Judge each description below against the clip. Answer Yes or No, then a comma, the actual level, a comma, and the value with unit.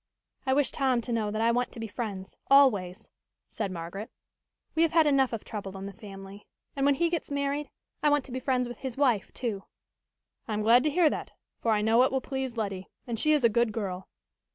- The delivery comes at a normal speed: No, fast, 230 wpm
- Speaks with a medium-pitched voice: No, high, 235 Hz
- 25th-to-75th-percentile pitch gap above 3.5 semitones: Yes, average, 4.7 semitones